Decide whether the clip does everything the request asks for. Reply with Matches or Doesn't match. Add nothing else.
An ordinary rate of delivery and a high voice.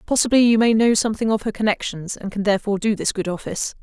Doesn't match